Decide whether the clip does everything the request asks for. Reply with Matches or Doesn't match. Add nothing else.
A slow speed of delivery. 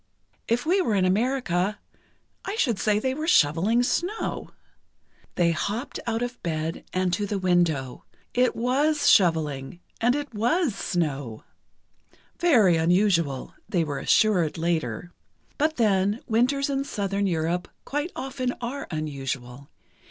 Matches